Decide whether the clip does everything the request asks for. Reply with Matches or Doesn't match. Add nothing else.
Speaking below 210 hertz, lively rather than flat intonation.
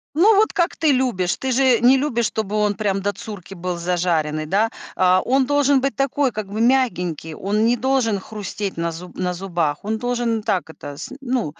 Doesn't match